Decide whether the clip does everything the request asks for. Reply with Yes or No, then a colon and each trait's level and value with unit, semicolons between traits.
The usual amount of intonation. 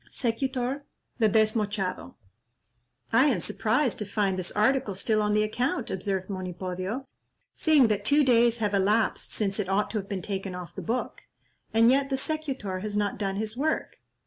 Yes: average, 4.1 semitones